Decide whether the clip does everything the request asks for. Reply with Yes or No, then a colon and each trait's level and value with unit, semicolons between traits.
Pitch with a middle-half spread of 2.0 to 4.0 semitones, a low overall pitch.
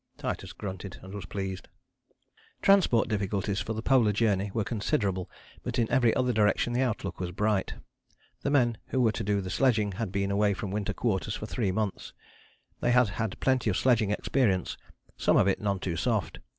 Yes: average, 3.3 semitones; low, 105 Hz